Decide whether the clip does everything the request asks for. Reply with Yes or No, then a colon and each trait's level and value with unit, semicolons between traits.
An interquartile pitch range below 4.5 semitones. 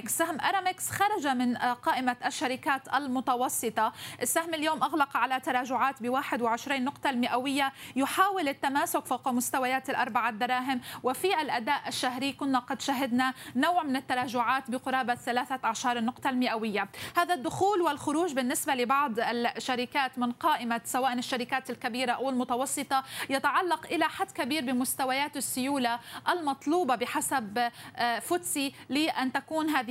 Yes: average, 2.8 semitones